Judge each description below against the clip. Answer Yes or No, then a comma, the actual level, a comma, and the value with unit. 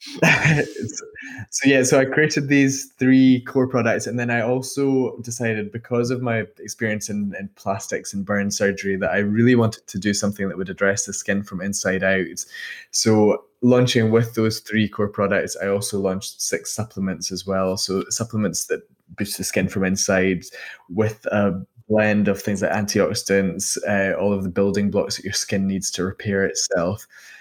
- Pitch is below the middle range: Yes, low, 105 Hz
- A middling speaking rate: Yes, average, 180 wpm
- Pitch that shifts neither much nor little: Yes, average, 3.2 semitones